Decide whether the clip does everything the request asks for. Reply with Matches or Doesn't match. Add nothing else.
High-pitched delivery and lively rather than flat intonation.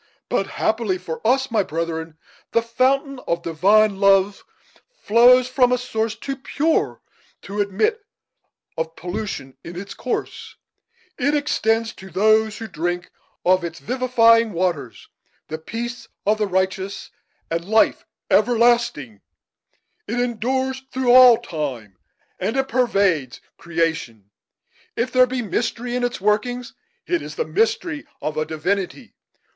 Matches